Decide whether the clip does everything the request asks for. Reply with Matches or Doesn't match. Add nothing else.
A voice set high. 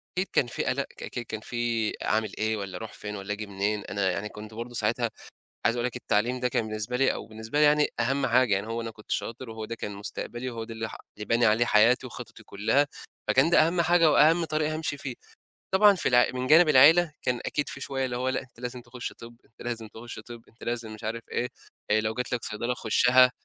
Doesn't match